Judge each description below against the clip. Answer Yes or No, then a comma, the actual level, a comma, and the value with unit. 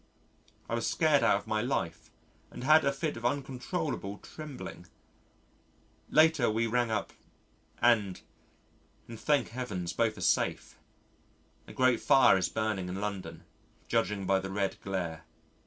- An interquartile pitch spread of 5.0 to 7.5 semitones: Yes, wide, 5.4 semitones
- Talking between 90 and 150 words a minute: Yes, average, 140 wpm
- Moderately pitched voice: No, low, 110 Hz